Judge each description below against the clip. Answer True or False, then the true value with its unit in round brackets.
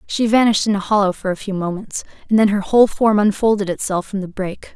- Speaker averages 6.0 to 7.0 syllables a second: True (6.5 syllables/s)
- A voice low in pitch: False (205 Hz)